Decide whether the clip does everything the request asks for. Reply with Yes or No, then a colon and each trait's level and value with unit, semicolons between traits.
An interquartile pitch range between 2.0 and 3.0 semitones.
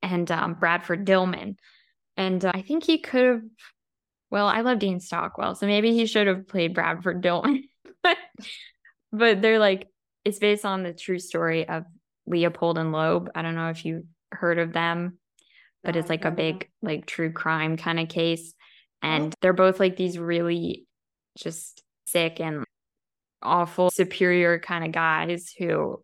No: average, 3.4 semitones